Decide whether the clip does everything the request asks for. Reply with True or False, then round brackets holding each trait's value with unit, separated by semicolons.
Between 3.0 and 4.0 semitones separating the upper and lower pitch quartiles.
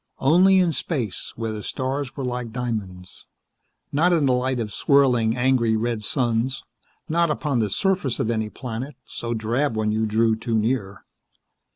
True (3.7 semitones)